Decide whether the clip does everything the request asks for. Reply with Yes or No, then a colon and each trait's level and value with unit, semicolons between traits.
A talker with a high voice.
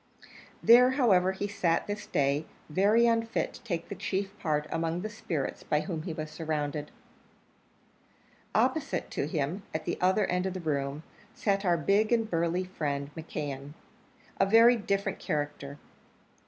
No: medium, 175 Hz